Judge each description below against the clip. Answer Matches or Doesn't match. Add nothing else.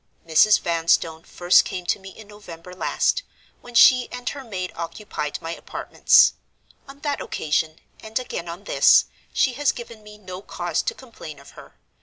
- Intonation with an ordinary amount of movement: Doesn't match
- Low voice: Doesn't match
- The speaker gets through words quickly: Doesn't match